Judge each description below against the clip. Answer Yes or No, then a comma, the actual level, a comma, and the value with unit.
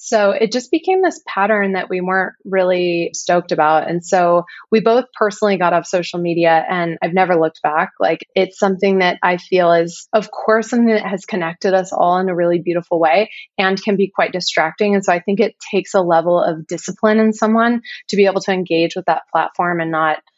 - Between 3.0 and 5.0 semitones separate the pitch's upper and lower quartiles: Yes, average, 3.4 semitones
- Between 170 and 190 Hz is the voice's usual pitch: Yes, medium, 185 Hz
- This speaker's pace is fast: Yes, fast, 215 wpm